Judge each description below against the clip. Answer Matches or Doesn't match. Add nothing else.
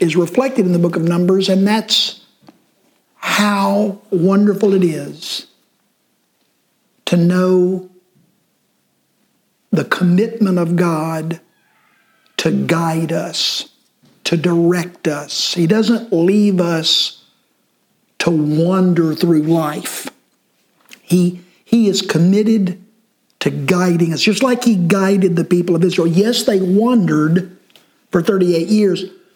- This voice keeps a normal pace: Doesn't match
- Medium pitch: Matches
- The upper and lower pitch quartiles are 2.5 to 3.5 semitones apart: Matches